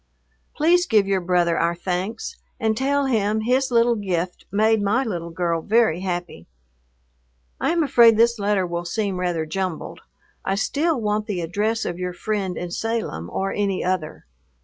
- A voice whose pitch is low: No, high, 200 Hz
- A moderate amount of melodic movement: Yes, average, 4.3 semitones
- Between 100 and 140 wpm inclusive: No, average, 165 wpm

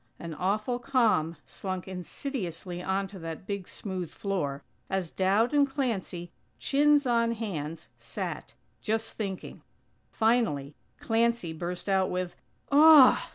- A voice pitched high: Yes, high, 195 Hz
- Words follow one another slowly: Yes, slow, 115 wpm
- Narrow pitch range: No, average, 5.0 semitones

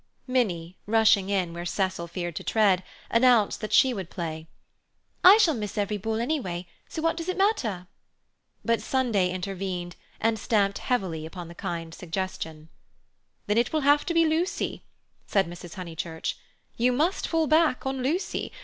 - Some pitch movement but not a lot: No, wide, 6.7 semitones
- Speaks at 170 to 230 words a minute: No, average, 160 wpm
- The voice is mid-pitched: No, high, 205 Hz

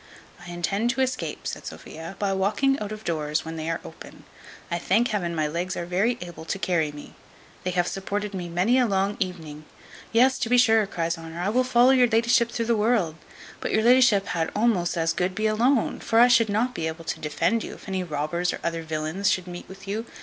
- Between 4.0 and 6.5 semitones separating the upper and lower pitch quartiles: Yes, average, 5.2 semitones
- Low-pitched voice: No, high, 195 Hz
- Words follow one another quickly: Yes, fast, 230 wpm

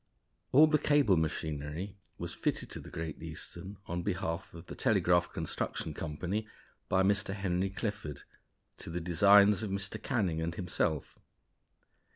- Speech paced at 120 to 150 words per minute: Yes, average, 145 wpm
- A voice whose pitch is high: No, very low, 90 Hz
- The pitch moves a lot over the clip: No, average, 3.8 semitones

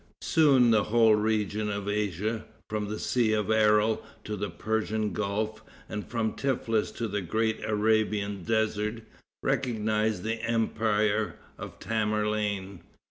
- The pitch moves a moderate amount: No, narrow, 1.0 semitones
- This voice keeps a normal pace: No, slow, 130 wpm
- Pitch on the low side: Yes, low, 110 Hz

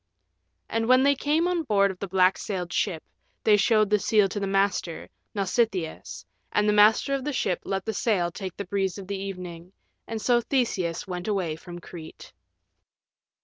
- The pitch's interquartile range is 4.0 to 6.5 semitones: No, average, 3.4 semitones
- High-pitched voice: Yes, high, 200 Hz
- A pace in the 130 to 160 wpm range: No, average, 185 wpm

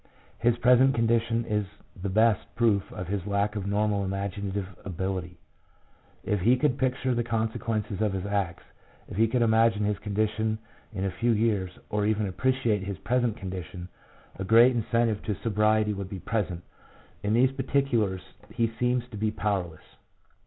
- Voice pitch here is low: Yes, low, 105 Hz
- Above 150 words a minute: Yes, average, 160 wpm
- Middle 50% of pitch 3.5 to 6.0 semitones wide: No, average, 2.9 semitones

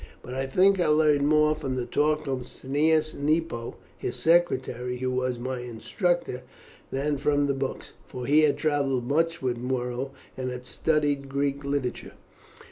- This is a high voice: No, medium, 140 Hz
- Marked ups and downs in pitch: No, average, 3.1 semitones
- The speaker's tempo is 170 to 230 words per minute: No, average, 160 wpm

